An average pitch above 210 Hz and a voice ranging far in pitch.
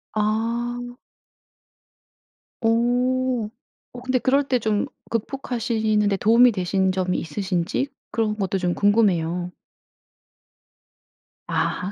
No: high, 220 Hz; average, 4.0 semitones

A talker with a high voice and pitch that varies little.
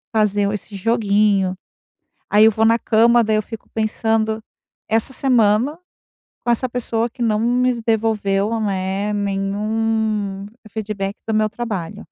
Yes: high, 215 Hz; narrow, 1.9 semitones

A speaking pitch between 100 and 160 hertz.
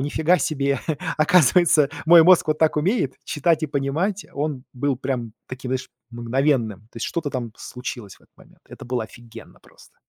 Yes: medium, 140 Hz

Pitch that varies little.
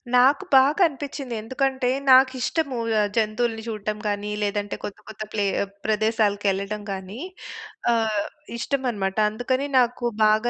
No: average, 3.7 semitones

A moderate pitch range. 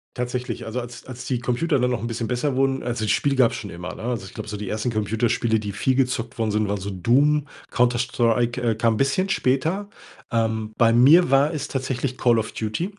Yes: average, 3.0 semitones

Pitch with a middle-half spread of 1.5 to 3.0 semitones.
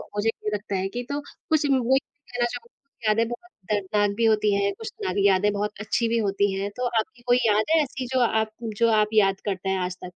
No: average, 3.5 semitones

